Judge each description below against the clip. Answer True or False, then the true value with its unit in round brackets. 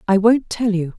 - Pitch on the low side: False (205 Hz)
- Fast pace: True (245 wpm)